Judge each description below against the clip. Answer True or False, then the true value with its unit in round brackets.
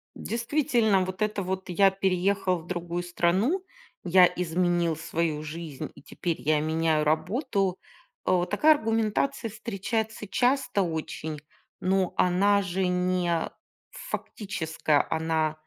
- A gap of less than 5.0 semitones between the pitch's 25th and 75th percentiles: True (3.7 semitones)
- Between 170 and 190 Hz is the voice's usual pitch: True (185 Hz)